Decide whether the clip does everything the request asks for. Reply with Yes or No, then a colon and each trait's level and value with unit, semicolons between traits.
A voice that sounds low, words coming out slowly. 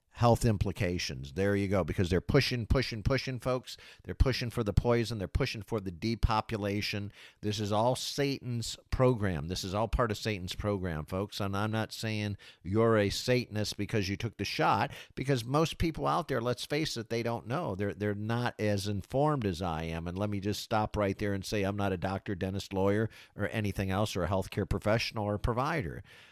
No: low, 105 Hz; fast, 205 wpm